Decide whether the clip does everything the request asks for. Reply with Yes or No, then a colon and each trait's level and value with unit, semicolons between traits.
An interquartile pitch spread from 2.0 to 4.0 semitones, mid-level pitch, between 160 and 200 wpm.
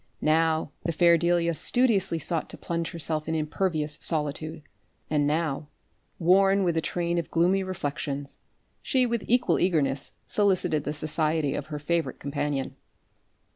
No: average, 2.7 semitones; medium, 165 Hz; average, 140 wpm